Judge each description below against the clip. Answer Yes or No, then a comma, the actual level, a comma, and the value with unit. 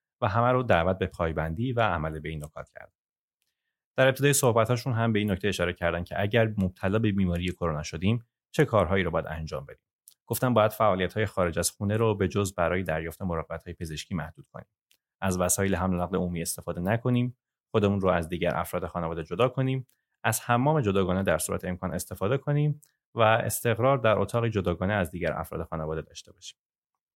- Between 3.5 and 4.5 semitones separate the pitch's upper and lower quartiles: No, average, 4.9 semitones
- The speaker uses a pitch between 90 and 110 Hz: Yes, very low, 95 Hz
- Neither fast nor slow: No, fast, 190 wpm